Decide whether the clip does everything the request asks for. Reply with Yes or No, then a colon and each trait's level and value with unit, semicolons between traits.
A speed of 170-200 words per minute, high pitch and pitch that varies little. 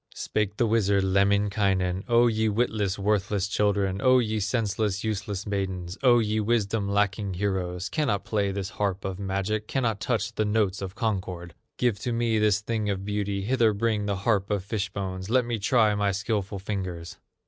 No: average, 175 wpm; low, 100 Hz; narrow, 2.1 semitones